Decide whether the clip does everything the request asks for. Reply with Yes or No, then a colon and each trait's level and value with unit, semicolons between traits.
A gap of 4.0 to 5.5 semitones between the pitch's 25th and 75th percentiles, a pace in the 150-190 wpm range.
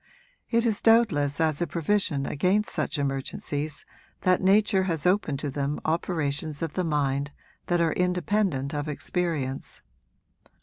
No: average, 4.6 semitones; slow, 135 wpm